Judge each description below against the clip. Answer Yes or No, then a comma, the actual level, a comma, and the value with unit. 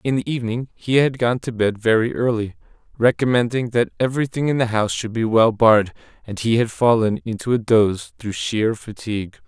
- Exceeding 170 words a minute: Yes, average, 190 wpm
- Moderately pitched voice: No, low, 115 Hz